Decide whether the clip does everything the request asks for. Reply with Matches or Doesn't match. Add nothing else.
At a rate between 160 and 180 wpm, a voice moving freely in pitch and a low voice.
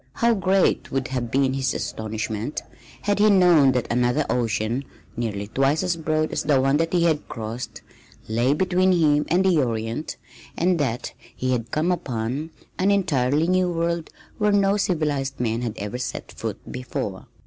Doesn't match